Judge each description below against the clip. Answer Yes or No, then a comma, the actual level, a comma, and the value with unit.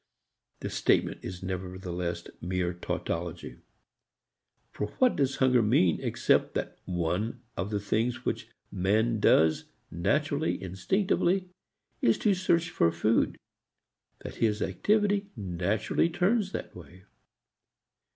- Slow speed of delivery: Yes, slow, 110 wpm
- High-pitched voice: No, low, 105 Hz